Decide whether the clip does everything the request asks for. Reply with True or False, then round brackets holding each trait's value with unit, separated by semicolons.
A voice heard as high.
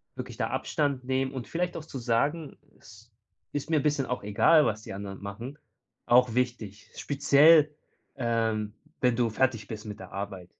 False (125 Hz)